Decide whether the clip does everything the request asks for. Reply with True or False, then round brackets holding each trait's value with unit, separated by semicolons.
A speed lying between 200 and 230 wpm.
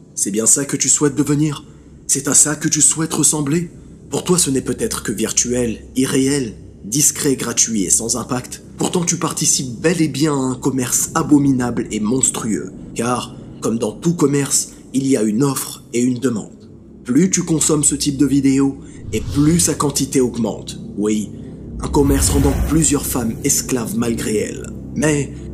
False (175 wpm)